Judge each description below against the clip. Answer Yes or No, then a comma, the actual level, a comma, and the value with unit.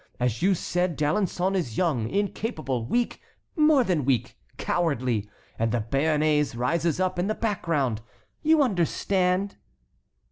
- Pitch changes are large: Yes, wide, 7.1 semitones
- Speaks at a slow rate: Yes, slow, 130 wpm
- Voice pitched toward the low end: No, medium, 165 Hz